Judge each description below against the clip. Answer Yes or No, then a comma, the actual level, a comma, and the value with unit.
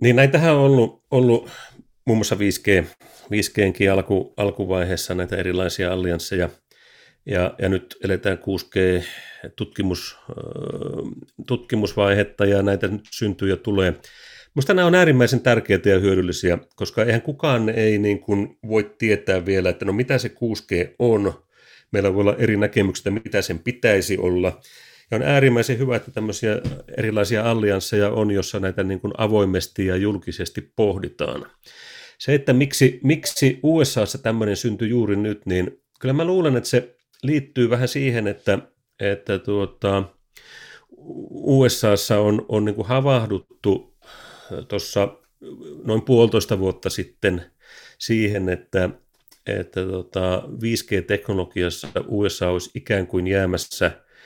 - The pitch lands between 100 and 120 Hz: Yes, low, 105 Hz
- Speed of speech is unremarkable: Yes, average, 130 wpm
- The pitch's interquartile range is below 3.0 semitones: No, average, 3.9 semitones